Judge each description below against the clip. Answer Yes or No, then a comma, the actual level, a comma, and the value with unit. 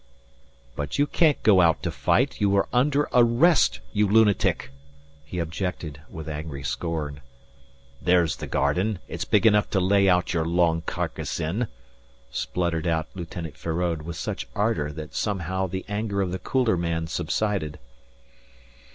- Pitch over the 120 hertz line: No, very low, 90 Hz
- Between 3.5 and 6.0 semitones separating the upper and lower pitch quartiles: Yes, average, 4.4 semitones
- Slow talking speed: No, average, 150 wpm